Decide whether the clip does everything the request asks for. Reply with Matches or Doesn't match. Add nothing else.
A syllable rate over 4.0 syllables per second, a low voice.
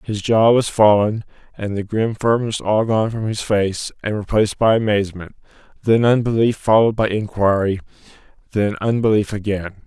Matches